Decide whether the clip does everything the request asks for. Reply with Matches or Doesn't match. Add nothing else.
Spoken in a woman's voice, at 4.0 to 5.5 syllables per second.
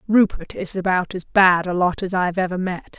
Matches